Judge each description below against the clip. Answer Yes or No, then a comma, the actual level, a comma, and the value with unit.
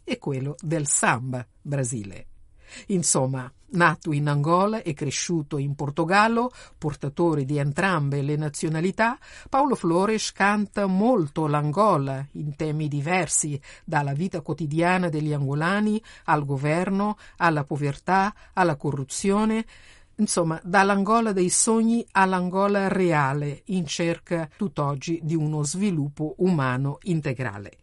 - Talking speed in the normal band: No, slow, 110 wpm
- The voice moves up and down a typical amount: Yes, average, 4.9 semitones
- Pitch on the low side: No, medium, 165 Hz